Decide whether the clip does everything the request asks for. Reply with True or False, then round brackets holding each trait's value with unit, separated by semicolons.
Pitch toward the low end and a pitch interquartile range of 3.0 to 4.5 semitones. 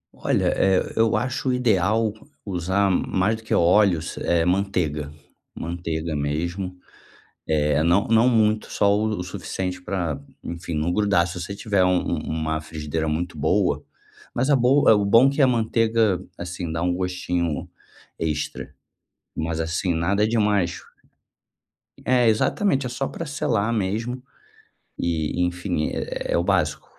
False (95 Hz; 4.9 semitones)